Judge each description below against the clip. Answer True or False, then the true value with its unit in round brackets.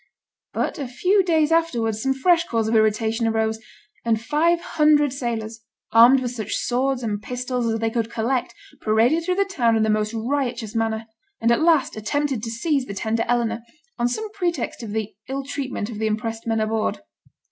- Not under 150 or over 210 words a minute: True (190 wpm)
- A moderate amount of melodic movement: True (4.1 semitones)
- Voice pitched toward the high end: True (235 Hz)